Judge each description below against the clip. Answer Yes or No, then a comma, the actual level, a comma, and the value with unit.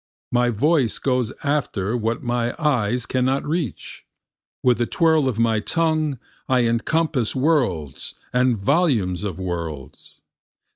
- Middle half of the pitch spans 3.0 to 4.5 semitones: No, average, 5.2 semitones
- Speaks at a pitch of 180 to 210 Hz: No, low, 125 Hz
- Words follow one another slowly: Yes, slow, 125 wpm